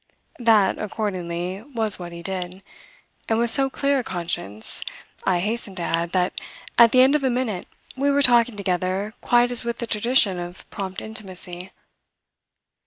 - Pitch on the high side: Yes, high, 205 Hz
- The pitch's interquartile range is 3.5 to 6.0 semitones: Yes, average, 4.8 semitones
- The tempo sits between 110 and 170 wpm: Yes, average, 165 wpm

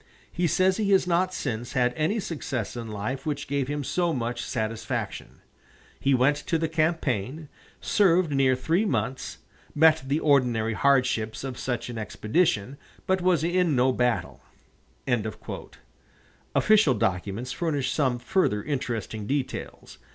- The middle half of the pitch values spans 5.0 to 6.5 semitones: Yes, average, 5.3 semitones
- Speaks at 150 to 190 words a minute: No, slow, 135 wpm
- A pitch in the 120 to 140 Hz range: Yes, low, 135 Hz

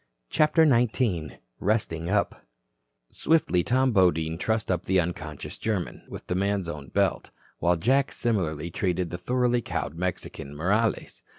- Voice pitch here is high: No, very low, 95 Hz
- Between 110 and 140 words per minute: Yes, slow, 135 wpm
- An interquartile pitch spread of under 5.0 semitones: No, wide, 5.5 semitones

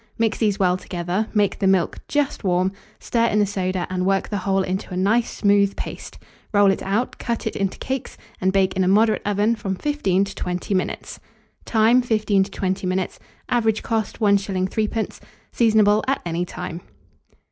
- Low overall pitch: No, high, 200 Hz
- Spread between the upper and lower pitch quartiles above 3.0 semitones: No, average, 2.7 semitones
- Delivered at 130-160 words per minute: No, average, 180 wpm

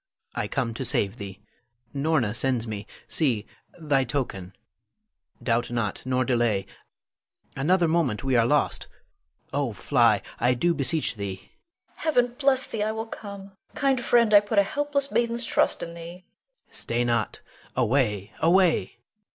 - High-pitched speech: No, low, 135 Hz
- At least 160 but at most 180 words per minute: No, average, 150 wpm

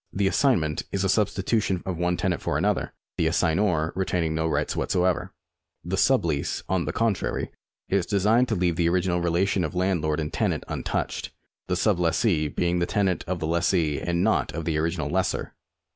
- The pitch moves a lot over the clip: No, average, 2.9 semitones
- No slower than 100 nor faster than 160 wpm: No, average, 190 wpm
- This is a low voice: Yes, very low, 90 Hz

